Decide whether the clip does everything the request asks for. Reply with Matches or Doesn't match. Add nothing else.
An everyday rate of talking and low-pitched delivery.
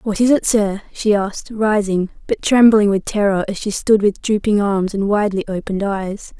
Doesn't match